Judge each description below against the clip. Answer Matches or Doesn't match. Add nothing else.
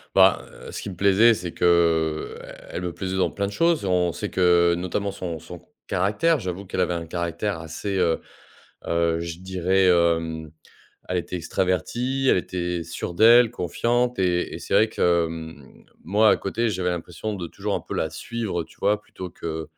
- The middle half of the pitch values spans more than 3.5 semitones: Doesn't match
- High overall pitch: Doesn't match